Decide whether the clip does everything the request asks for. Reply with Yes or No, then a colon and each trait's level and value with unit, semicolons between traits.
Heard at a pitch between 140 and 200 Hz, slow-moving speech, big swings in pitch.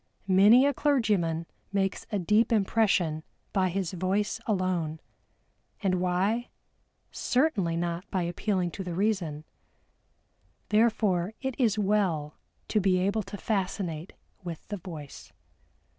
No: high, 190 Hz; slow, 120 wpm; average, 3.5 semitones